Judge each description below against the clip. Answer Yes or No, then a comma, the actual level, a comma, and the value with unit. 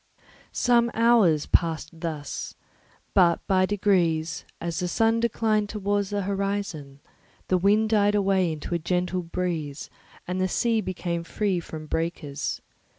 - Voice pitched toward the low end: No, medium, 185 Hz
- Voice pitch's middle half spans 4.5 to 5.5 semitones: No, average, 3.6 semitones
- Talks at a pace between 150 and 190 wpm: No, slow, 135 wpm